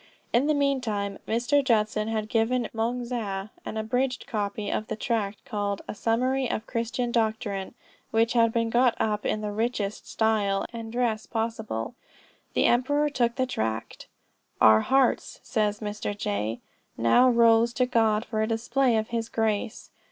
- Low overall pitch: No, high, 225 Hz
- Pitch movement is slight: Yes, narrow, 2.3 semitones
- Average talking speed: Yes, average, 160 wpm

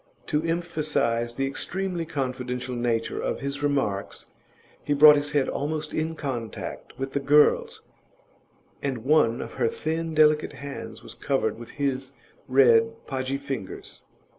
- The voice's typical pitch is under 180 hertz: Yes, medium, 140 Hz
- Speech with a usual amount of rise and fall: Yes, average, 3.5 semitones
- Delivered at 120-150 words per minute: Yes, average, 140 wpm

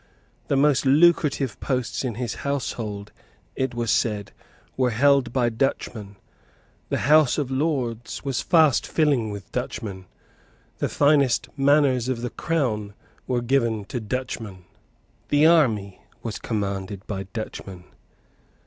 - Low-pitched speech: Yes, low, 125 Hz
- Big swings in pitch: No, average, 4.6 semitones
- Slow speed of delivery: Yes, slow, 125 wpm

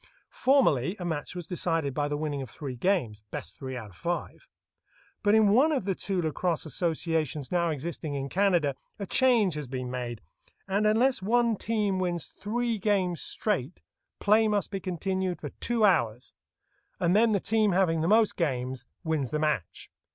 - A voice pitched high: No, medium, 175 Hz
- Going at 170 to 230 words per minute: Yes, average, 175 wpm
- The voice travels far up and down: Yes, wide, 5.9 semitones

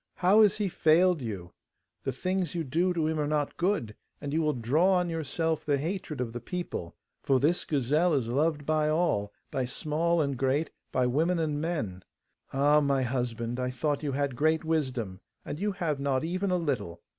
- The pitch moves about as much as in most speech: Yes, average, 4.5 semitones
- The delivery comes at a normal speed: Yes, average, 195 wpm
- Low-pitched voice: No, medium, 150 Hz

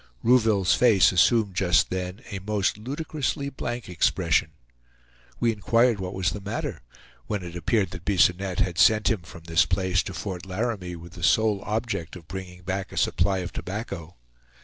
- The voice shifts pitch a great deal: No, average, 3.5 semitones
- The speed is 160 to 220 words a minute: Yes, average, 170 wpm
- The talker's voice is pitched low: Yes, very low, 95 Hz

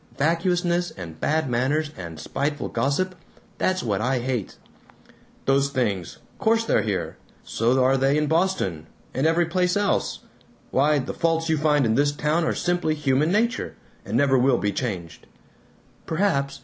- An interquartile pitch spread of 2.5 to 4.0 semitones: No, average, 5.0 semitones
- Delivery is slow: No, average, 155 wpm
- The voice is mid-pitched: Yes, medium, 145 Hz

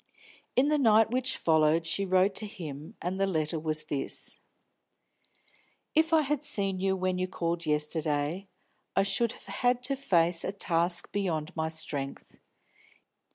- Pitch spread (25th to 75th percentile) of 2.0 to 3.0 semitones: No, average, 5.1 semitones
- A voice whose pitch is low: No, medium, 185 Hz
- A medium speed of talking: Yes, average, 155 wpm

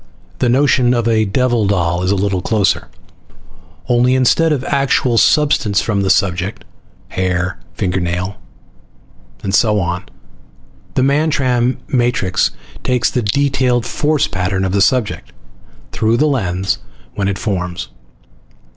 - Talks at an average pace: No, slow, 130 wpm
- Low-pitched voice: Yes, low, 110 Hz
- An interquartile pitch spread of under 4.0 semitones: No, average, 5.2 semitones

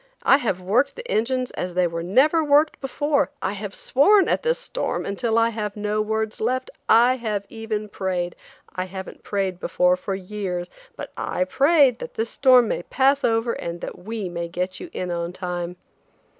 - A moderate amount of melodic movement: No, wide, 5.9 semitones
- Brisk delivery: No, average, 180 wpm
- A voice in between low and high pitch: No, high, 215 Hz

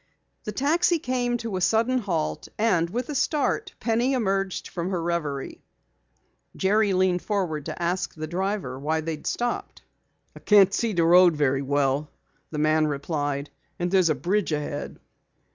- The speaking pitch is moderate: Yes, medium, 180 Hz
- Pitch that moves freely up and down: Yes, wide, 6.1 semitones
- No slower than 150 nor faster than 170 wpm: Yes, average, 160 wpm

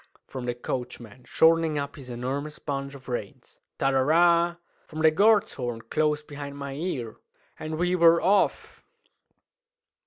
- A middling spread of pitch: Yes, average, 4.1 semitones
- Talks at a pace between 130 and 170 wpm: Yes, average, 155 wpm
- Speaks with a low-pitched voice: No, medium, 145 Hz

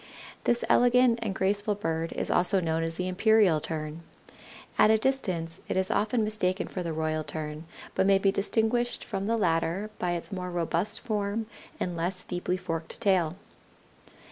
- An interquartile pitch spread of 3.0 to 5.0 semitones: Yes, average, 4.4 semitones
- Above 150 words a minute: Yes, average, 170 wpm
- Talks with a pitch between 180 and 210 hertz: Yes, medium, 185 Hz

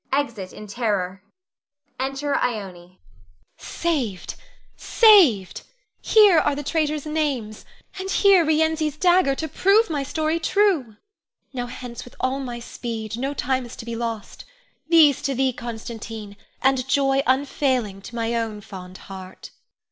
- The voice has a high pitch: Yes, very high, 260 Hz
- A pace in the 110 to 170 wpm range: Yes, average, 140 wpm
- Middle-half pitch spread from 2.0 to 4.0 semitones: No, average, 5.3 semitones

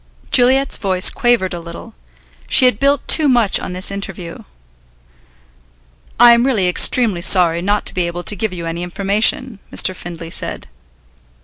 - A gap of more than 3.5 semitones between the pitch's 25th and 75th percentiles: Yes, wide, 5.4 semitones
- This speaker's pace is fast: No, average, 155 wpm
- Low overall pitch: No, high, 195 Hz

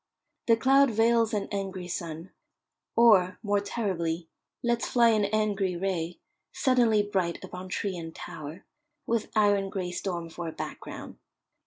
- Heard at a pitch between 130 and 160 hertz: No, high, 195 Hz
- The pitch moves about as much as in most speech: Yes, average, 3.9 semitones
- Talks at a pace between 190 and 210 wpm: No, average, 140 wpm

